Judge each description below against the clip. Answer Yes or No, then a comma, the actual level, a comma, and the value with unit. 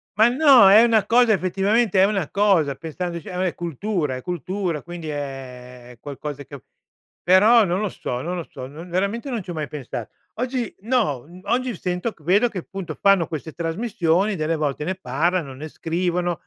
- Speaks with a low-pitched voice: No, medium, 180 Hz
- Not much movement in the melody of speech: No, average, 5.1 semitones